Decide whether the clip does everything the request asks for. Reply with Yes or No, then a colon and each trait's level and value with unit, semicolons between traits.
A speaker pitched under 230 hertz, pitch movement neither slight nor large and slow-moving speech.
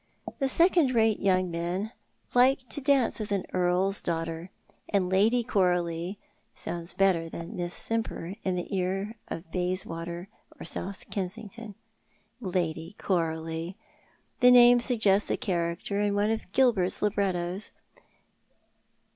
Yes: high, 190 Hz; average, 4.1 semitones; slow, 125 wpm